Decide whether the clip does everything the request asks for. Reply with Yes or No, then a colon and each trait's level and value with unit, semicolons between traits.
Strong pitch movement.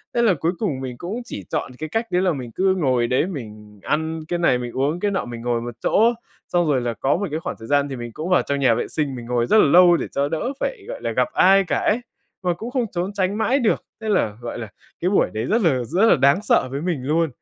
Yes: wide, 7.4 semitones